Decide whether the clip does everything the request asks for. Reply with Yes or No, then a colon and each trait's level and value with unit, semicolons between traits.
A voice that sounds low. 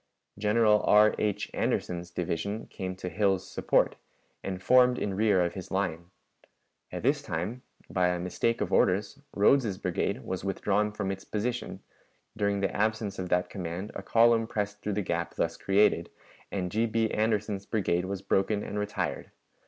Yes: low, 100 Hz